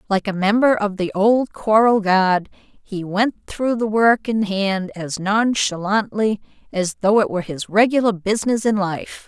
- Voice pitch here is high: Yes, high, 205 Hz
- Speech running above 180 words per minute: No, average, 170 wpm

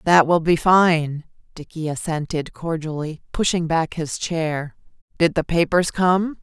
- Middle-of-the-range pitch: Yes, medium, 165 Hz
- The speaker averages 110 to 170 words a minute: Yes, average, 140 wpm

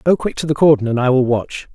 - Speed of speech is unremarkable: No, fast, 310 wpm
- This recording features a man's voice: Yes, male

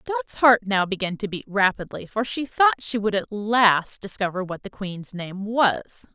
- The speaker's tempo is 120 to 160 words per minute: No, average, 195 wpm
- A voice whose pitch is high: Yes, high, 210 Hz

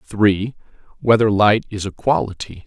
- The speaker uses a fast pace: No, slow, 135 wpm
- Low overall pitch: Yes, low, 100 Hz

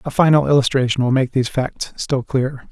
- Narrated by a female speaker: No, male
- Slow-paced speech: No, average, 200 wpm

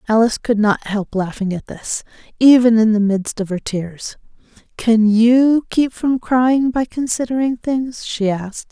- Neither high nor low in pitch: No, high, 230 Hz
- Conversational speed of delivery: Yes, average, 165 wpm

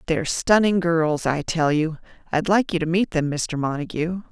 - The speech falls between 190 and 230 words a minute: No, average, 180 wpm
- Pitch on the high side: No, medium, 165 Hz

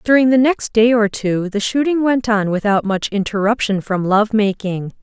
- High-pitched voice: Yes, high, 215 Hz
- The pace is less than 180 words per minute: No, average, 190 wpm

